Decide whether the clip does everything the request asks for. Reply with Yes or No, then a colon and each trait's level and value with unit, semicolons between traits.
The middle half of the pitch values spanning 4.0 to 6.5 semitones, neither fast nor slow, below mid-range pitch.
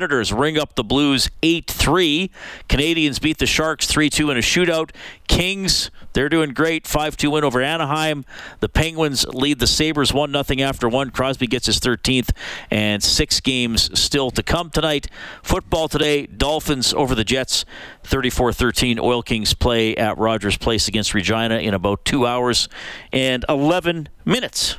Yes: average, 4.8 semitones; average, 150 wpm; low, 130 Hz